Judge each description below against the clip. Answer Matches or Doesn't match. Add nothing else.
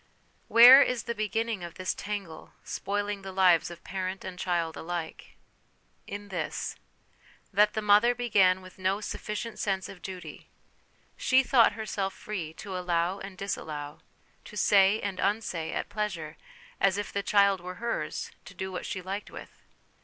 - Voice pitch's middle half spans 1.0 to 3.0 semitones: Matches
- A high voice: Matches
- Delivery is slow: Doesn't match